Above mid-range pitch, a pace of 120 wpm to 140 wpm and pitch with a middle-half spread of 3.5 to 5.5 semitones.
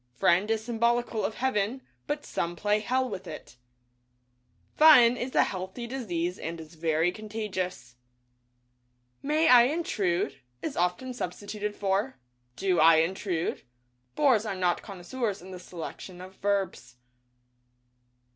Yes: high, 195 Hz; slow, 135 wpm; average, 5.2 semitones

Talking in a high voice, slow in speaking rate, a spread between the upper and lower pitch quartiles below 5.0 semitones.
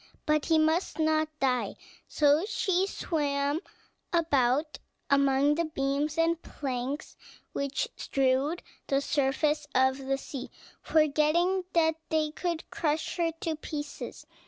Yes: very high, 300 Hz; slow, 120 wpm; narrow, 2.6 semitones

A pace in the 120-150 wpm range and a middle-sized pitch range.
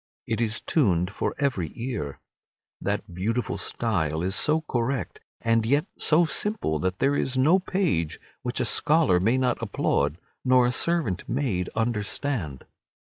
No: average, 145 wpm; wide, 7.5 semitones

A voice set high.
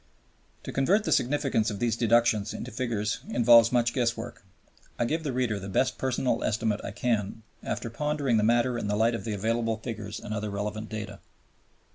No: low, 115 Hz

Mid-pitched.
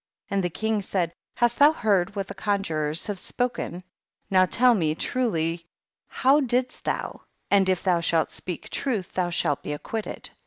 No: high, 195 Hz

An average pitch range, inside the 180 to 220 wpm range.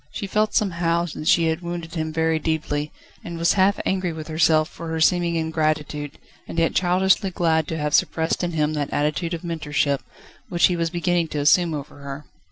No: narrow, 2.1 semitones; average, 195 wpm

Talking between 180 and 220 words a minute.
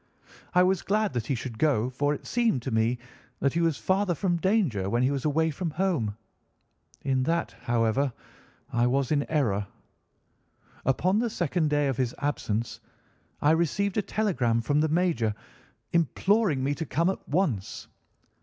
No: average, 165 wpm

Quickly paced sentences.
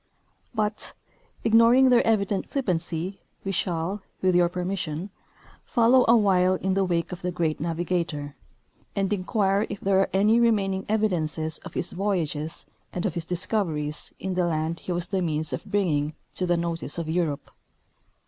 No: average, 160 wpm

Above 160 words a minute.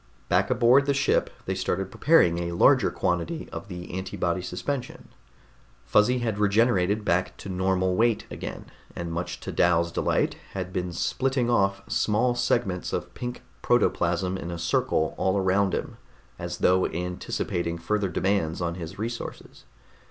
No: average, 150 wpm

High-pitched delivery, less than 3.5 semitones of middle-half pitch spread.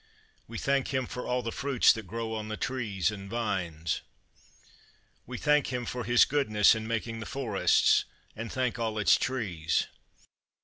No: low, 115 Hz; average, 3.0 semitones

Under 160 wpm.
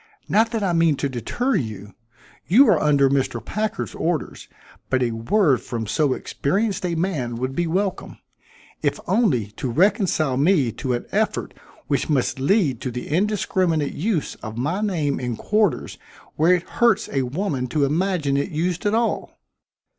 No: average, 165 wpm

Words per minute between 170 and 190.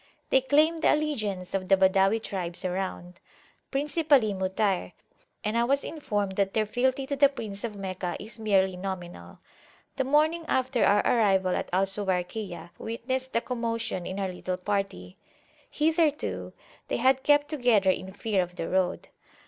No: average, 155 wpm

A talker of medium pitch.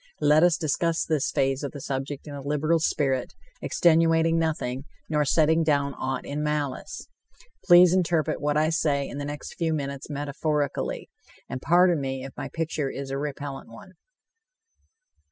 Yes: medium, 150 Hz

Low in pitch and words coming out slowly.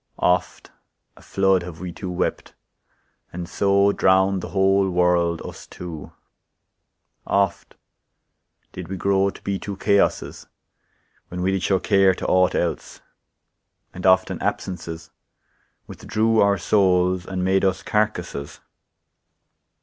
Yes: very low, 95 Hz; slow, 125 wpm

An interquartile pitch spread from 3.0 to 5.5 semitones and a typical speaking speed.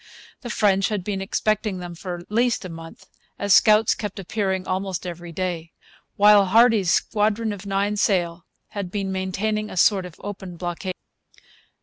No: narrow, 2.6 semitones; average, 160 wpm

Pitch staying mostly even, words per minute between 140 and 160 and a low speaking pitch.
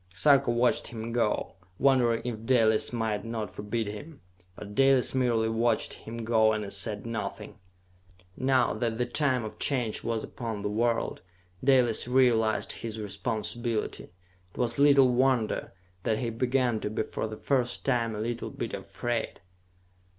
Yes: narrow, 2.2 semitones; average, 150 wpm; low, 115 Hz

